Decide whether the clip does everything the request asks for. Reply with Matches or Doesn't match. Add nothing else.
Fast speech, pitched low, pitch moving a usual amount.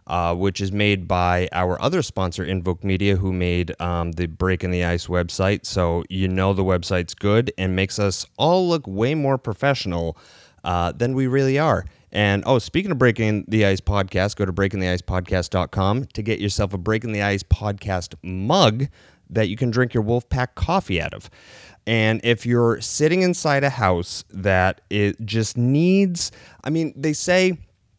Doesn't match